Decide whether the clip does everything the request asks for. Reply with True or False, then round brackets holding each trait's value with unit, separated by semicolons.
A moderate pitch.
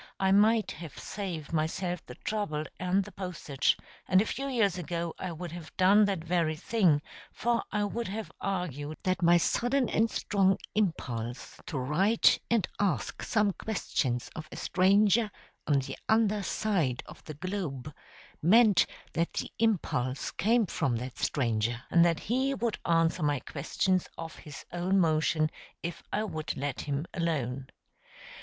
True (175 Hz)